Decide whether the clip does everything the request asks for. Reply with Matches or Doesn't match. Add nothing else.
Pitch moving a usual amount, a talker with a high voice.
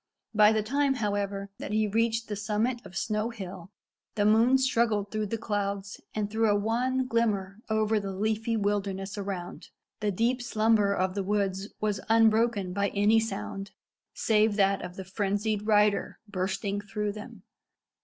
Doesn't match